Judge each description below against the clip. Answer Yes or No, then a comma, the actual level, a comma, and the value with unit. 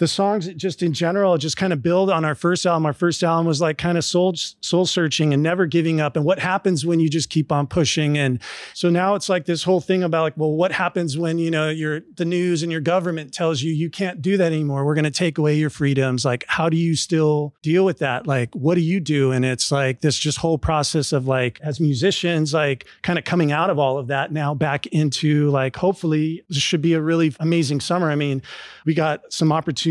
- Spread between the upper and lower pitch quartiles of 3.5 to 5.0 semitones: No, average, 2.8 semitones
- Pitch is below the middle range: No, medium, 160 Hz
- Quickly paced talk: Yes, fast, 245 wpm